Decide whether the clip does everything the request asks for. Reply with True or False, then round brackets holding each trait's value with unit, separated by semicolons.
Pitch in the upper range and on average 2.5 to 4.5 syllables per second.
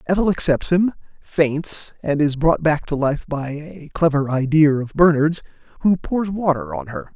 False (155 Hz; 4.3 syllables/s)